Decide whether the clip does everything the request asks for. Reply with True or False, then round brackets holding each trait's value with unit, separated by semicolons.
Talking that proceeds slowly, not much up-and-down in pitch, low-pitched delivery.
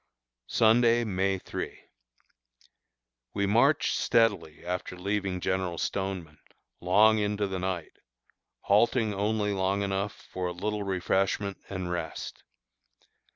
True (110 wpm; 2.3 semitones; 100 Hz)